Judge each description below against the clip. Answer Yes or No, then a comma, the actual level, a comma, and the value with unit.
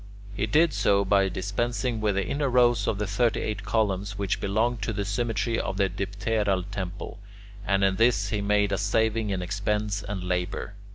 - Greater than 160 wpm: Yes, average, 185 wpm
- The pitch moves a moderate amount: No, narrow, 2.3 semitones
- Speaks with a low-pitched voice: Yes, low, 105 Hz